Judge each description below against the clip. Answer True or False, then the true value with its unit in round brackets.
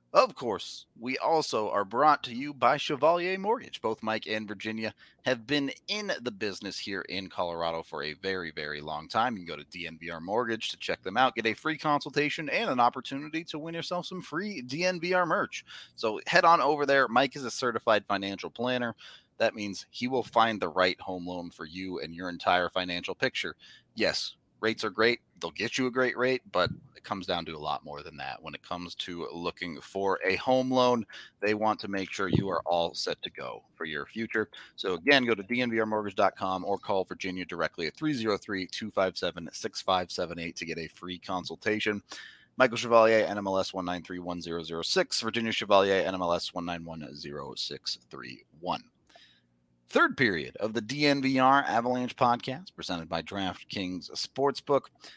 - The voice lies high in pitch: False (110 Hz)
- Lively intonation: True (6.3 semitones)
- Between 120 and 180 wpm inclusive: True (175 wpm)